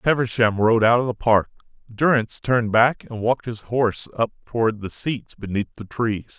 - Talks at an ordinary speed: Yes, average, 190 wpm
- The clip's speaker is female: No, male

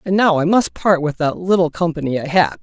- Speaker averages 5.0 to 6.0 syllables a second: Yes, 5.6 syllables/s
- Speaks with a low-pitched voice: No, medium, 170 Hz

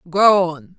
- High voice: No, medium, 180 Hz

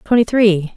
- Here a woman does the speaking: Yes, female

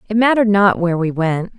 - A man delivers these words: No, female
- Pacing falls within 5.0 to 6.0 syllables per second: No, 6.3 syllables/s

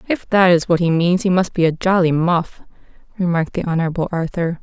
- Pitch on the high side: No, medium, 170 Hz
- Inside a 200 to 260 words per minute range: Yes, fast, 205 wpm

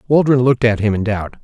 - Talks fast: Yes, fast, 250 wpm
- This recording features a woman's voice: No, male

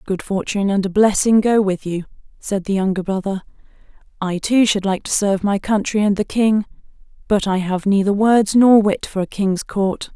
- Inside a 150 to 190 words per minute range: No, average, 200 wpm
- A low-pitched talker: No, high, 200 Hz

